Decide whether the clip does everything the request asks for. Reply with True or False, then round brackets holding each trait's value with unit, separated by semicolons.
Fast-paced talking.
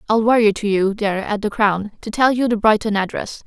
True (245 wpm)